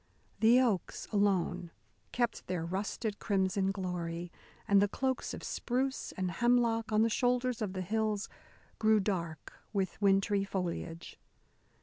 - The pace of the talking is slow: Yes, slow, 130 wpm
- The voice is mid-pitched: No, high, 200 Hz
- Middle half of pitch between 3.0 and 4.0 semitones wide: Yes, average, 3.4 semitones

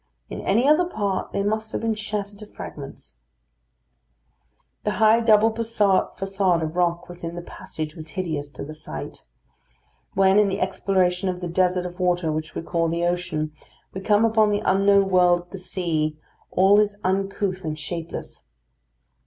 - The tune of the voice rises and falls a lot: No, average, 3.1 semitones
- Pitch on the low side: No, medium, 185 Hz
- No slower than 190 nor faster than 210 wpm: No, average, 165 wpm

